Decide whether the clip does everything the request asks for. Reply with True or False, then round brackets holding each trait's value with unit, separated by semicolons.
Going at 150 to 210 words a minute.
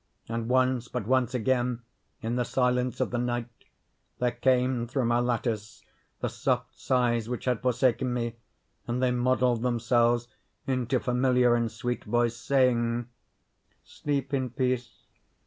False (135 wpm)